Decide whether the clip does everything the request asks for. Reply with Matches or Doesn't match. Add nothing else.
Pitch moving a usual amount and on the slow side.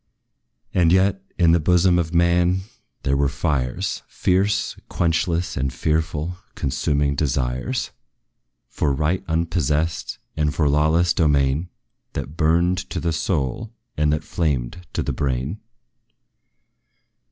Matches